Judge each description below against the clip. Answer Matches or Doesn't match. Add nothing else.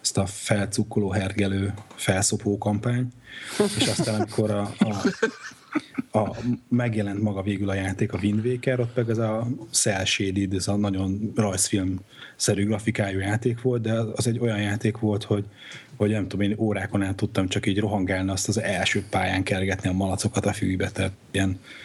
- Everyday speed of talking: Doesn't match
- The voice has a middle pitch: Doesn't match